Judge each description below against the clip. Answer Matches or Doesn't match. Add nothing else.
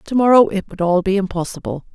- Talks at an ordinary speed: Doesn't match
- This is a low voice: Doesn't match